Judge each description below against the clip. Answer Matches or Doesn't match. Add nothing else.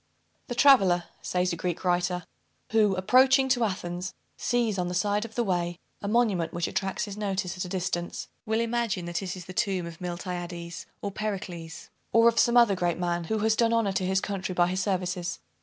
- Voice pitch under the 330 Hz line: Matches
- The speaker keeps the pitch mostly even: Doesn't match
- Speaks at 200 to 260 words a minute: Matches